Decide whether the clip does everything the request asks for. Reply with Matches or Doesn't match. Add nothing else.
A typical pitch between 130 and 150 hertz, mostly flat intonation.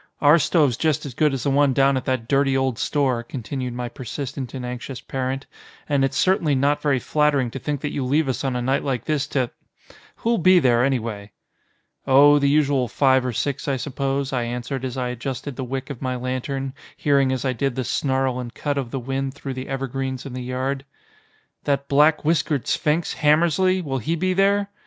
Matches